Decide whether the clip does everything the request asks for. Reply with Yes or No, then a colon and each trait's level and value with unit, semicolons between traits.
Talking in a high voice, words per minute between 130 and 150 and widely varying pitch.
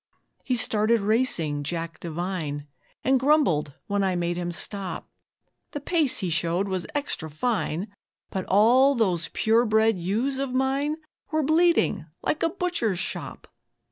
Yes: high, 210 Hz; average, 140 wpm; wide, 7.3 semitones